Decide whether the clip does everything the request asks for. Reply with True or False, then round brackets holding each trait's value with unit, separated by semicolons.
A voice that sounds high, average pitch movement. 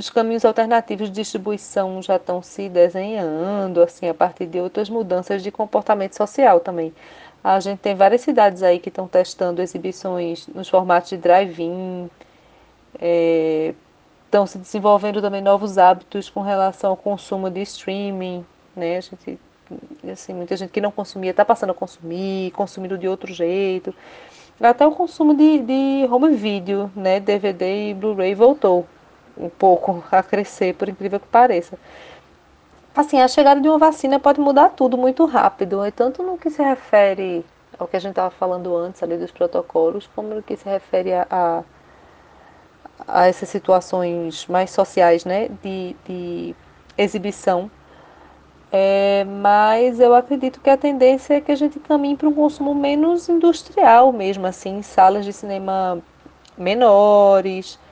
True (195 Hz; 4.1 semitones)